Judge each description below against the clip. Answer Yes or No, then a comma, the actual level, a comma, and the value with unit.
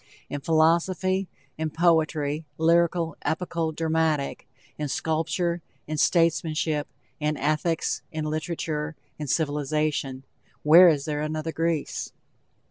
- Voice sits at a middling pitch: Yes, medium, 160 Hz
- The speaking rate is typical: No, slow, 105 wpm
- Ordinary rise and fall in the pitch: No, narrow, 1.6 semitones